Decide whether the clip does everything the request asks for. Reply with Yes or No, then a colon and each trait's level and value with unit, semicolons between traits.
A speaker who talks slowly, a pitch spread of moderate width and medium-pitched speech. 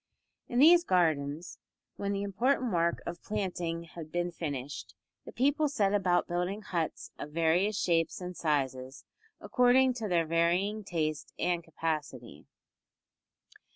Yes: slow, 130 wpm; average, 4.3 semitones; medium, 175 Hz